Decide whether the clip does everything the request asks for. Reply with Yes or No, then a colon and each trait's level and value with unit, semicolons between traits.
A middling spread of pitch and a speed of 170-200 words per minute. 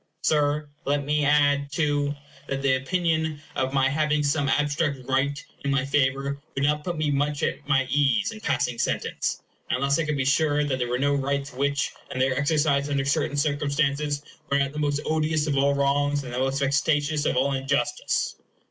No: narrow, 1.3 semitones; average, 190 wpm